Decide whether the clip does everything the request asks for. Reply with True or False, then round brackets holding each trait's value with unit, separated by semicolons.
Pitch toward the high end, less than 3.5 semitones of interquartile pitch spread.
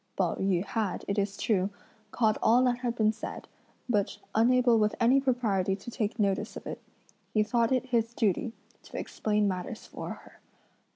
True (220 Hz; 3.1 semitones)